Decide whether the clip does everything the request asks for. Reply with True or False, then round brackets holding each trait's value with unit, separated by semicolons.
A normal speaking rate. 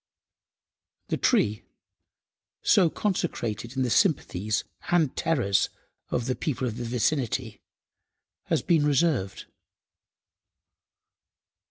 False (90 wpm)